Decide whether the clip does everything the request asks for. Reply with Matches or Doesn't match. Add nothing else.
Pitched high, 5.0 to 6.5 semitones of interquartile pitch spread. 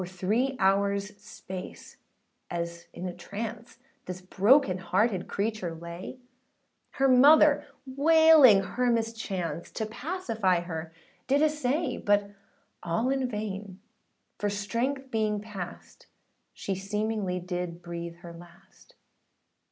Matches